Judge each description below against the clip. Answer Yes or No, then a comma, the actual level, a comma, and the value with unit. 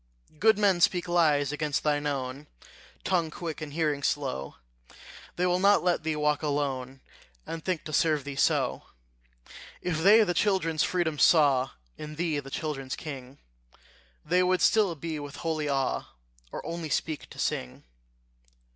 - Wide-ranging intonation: No, average, 3.3 semitones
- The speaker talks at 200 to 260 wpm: No, average, 155 wpm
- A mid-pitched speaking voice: Yes, medium, 155 Hz